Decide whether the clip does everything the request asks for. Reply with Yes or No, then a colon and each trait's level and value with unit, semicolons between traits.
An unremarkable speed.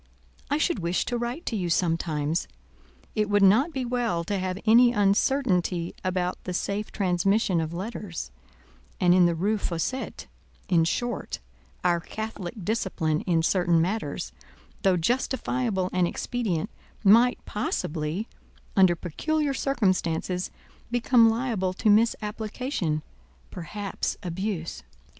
No: slow, 110 wpm